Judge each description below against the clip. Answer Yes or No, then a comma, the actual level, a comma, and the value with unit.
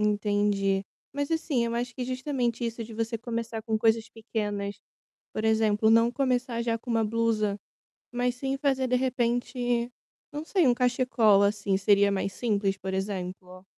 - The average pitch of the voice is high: Yes, high, 230 Hz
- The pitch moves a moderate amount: Yes, average, 3.1 semitones